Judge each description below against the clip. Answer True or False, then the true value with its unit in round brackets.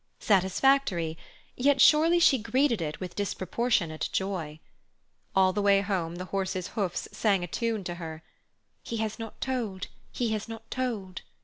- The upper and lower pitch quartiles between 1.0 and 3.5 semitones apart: False (4.2 semitones)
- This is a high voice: True (200 Hz)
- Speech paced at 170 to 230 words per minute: False (150 wpm)